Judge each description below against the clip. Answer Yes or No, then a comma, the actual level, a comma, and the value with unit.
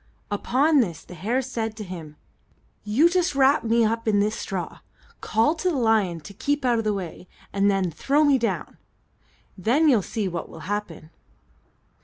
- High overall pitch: Yes, high, 220 Hz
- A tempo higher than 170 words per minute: Yes, average, 180 wpm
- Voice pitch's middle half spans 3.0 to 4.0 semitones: No, wide, 5.4 semitones